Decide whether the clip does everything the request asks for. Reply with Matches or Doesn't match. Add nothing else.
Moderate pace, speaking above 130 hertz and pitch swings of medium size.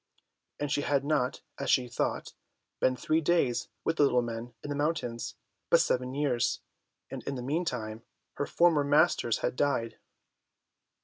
Matches